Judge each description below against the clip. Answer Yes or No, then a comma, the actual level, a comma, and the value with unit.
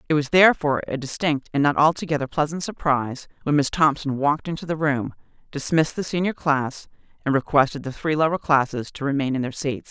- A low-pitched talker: No, medium, 145 Hz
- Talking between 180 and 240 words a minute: Yes, average, 195 wpm